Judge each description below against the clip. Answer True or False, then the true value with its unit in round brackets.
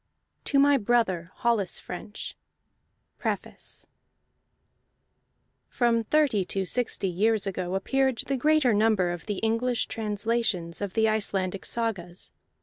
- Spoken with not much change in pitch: False (3.9 semitones)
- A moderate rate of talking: False (120 wpm)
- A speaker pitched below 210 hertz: False (220 Hz)